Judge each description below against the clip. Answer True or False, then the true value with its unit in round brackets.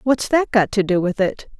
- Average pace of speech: False (265 wpm)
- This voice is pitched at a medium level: False (215 Hz)